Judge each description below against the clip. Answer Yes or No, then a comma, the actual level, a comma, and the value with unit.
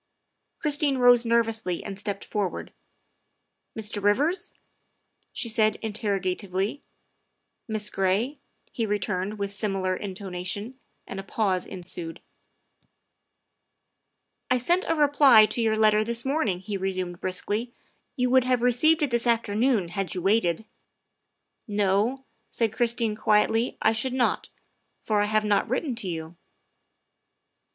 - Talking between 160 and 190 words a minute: No, average, 145 wpm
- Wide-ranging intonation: No, average, 3.8 semitones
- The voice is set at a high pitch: Yes, high, 215 Hz